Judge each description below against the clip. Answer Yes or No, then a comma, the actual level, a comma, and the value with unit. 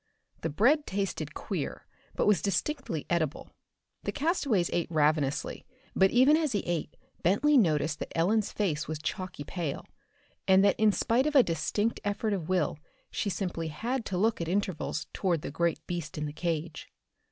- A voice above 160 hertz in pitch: Yes, medium, 185 Hz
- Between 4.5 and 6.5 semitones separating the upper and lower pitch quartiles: Yes, average, 5.2 semitones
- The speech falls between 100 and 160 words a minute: No, average, 170 wpm